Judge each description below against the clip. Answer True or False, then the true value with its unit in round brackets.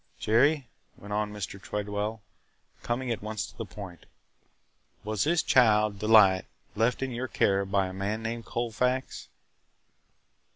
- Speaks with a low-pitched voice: True (110 Hz)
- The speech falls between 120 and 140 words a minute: True (135 wpm)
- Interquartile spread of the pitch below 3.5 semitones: True (2.8 semitones)